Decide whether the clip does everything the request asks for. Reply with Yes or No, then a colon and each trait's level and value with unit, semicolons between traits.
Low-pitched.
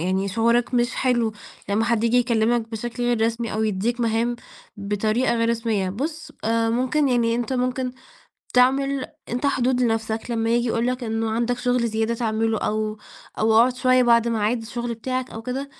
No: high, 235 Hz